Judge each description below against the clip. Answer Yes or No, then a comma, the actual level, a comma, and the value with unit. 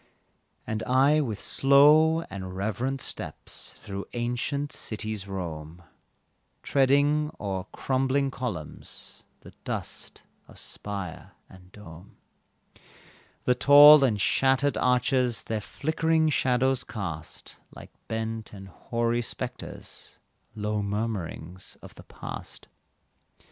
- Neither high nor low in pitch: No, low, 120 Hz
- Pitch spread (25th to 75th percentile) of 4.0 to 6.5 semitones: Yes, wide, 5.4 semitones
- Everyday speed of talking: No, slow, 100 wpm